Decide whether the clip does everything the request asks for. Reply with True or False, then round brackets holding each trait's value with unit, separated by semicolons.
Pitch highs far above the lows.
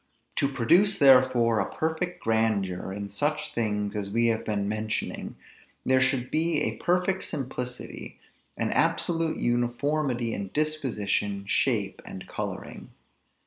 True (6.0 semitones)